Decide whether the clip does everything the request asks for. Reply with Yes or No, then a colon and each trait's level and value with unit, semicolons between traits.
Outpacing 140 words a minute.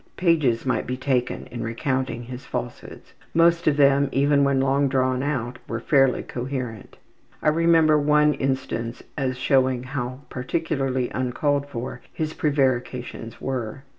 No: slow, 135 wpm